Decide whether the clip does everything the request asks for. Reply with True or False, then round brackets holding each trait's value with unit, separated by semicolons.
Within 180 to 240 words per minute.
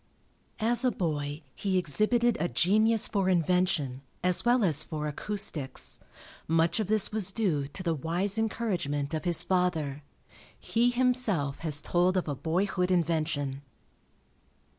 False (140 wpm)